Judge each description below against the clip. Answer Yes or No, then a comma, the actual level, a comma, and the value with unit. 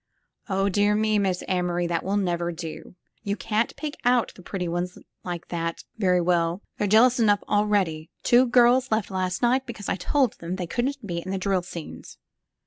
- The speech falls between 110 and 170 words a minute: No, average, 190 wpm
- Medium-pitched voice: No, high, 195 Hz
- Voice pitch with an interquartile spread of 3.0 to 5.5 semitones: Yes, average, 3.9 semitones